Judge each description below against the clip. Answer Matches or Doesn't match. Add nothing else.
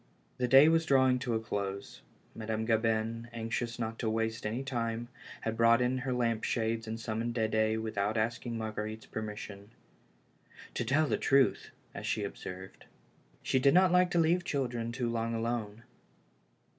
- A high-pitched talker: Doesn't match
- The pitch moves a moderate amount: Doesn't match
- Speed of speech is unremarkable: Matches